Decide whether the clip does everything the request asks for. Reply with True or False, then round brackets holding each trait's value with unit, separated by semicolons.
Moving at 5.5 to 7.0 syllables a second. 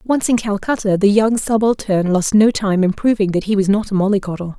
True (5.6 syllables/s)